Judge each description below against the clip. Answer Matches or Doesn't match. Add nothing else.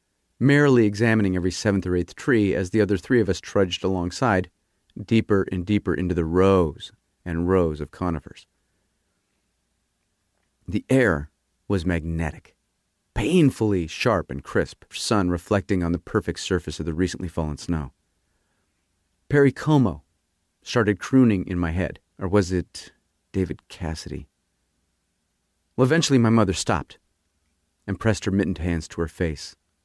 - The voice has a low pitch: Matches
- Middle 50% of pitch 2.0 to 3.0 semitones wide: Doesn't match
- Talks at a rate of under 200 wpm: Matches